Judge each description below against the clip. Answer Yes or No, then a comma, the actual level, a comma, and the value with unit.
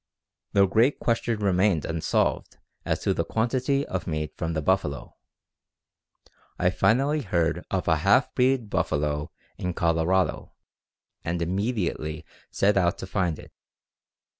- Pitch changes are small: No, average, 5.1 semitones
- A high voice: No, very low, 95 Hz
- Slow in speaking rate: Yes, slow, 130 wpm